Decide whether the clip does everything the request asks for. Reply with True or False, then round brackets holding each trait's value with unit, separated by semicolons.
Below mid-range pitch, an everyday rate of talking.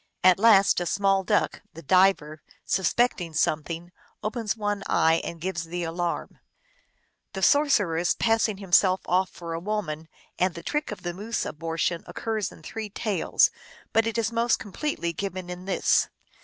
False (185 Hz; 160 wpm)